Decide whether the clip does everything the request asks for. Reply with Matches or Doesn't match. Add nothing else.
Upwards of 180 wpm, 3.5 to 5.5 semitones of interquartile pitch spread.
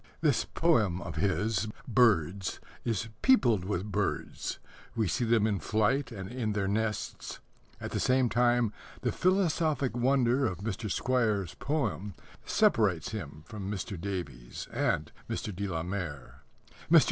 Doesn't match